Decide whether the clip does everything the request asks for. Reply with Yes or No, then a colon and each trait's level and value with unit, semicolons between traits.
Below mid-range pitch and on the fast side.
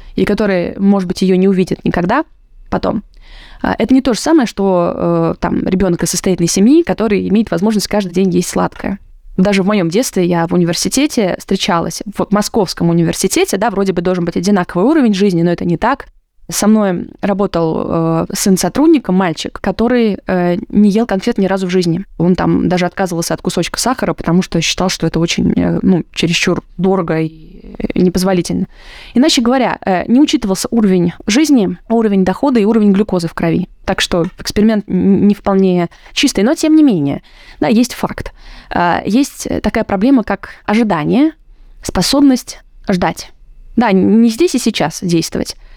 No: high, 195 Hz; fast, 170 wpm